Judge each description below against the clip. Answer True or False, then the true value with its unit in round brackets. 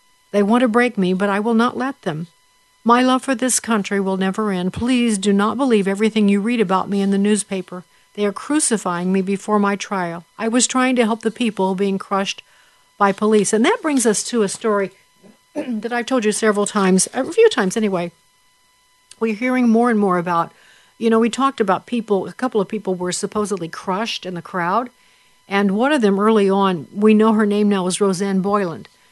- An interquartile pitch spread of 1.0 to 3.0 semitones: False (3.6 semitones)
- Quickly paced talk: True (210 wpm)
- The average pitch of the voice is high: True (210 Hz)